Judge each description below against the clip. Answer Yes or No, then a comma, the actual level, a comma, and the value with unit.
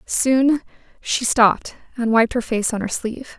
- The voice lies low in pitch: No, high, 235 Hz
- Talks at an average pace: Yes, average, 175 wpm